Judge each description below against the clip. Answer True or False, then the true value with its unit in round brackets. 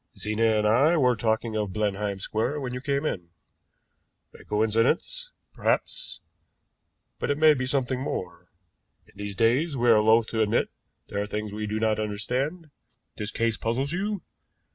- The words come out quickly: False (165 wpm)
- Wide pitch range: False (4.4 semitones)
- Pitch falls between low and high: False (115 Hz)